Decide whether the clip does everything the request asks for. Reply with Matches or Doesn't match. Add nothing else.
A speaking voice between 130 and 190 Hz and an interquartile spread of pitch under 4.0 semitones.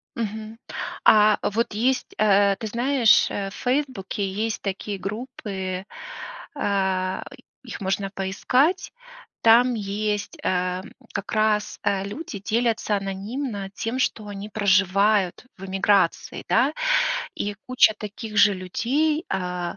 Doesn't match